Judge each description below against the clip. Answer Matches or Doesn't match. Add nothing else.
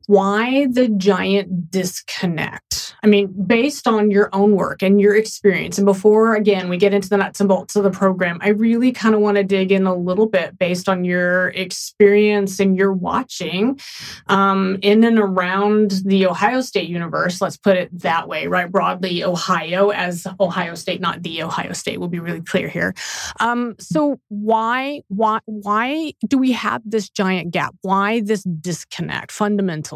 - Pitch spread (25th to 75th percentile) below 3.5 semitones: Matches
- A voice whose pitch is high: Matches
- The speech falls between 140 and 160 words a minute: Doesn't match